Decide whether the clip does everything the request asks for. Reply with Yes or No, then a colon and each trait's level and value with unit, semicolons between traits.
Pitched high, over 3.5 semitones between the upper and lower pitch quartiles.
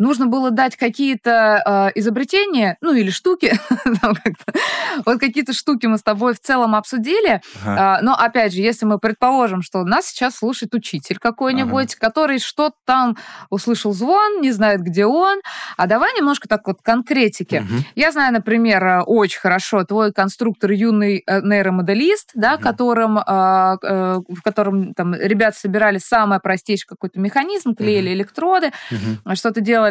Yes: high, 225 Hz; average, 4.7 semitones